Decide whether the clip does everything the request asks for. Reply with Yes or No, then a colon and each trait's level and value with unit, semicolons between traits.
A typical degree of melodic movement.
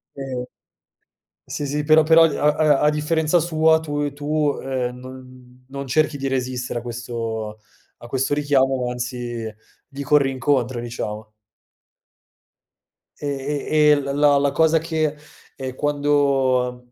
Yes: average, 3.0 semitones